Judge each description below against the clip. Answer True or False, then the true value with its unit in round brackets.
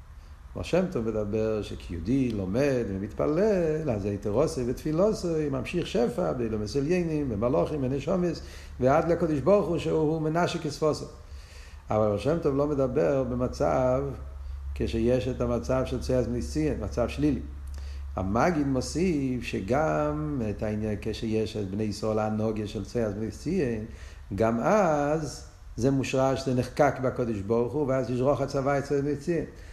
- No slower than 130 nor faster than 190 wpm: True (135 wpm)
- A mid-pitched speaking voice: False (125 Hz)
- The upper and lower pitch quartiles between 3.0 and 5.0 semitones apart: False (5.4 semitones)